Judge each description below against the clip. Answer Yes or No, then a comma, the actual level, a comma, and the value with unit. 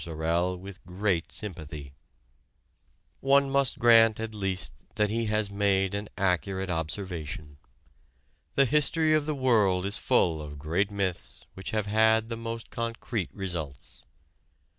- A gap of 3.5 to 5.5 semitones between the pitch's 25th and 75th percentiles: Yes, average, 4.3 semitones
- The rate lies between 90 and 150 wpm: Yes, slow, 135 wpm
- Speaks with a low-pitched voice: Yes, low, 100 Hz